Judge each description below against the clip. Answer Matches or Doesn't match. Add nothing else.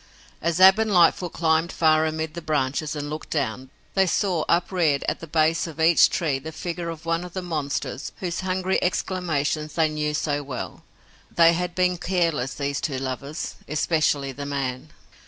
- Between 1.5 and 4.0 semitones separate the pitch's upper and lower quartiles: Matches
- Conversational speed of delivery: Matches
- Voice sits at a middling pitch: Matches